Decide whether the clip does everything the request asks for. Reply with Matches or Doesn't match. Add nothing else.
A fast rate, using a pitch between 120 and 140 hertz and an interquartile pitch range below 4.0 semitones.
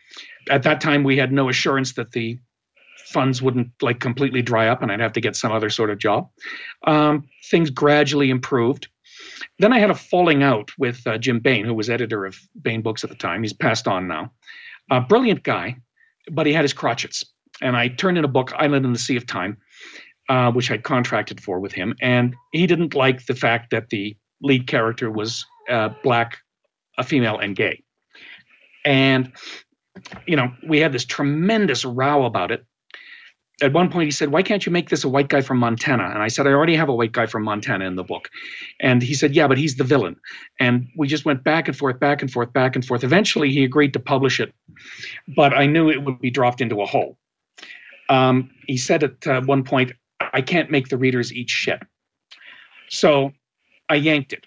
Matches